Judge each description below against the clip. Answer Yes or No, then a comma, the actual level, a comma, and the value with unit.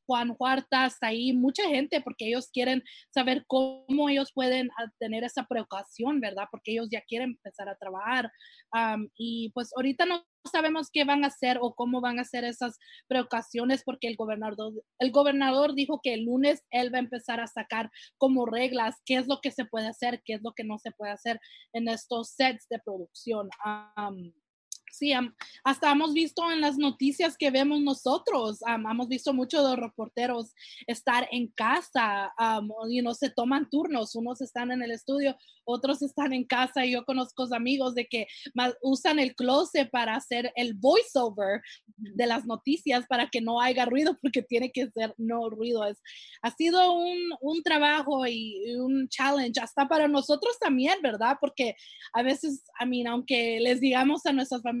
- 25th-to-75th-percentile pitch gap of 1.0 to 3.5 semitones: Yes, average, 3.0 semitones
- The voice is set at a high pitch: Yes, very high, 250 Hz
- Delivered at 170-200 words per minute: Yes, average, 180 wpm